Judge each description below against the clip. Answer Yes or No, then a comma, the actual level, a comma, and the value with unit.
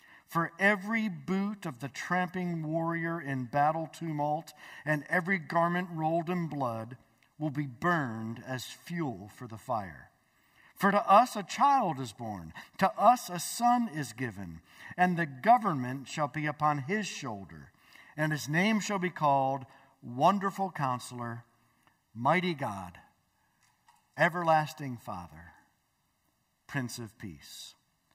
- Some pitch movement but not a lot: No, wide, 5.8 semitones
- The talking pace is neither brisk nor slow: No, slow, 130 wpm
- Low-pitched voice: No, medium, 155 Hz